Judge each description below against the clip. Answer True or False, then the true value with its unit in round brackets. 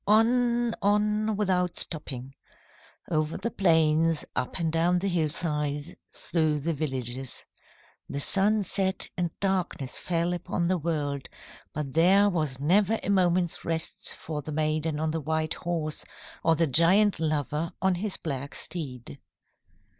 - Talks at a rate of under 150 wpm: True (140 wpm)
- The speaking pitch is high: False (165 Hz)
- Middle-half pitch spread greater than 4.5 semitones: False (3.8 semitones)